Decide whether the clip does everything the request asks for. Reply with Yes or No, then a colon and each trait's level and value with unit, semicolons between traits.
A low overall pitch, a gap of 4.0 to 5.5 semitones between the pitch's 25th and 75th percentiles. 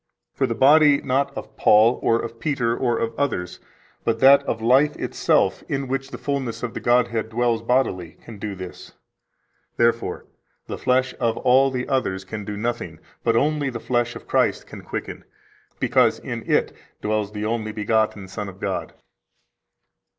No: low, 115 Hz; average, 3.4 semitones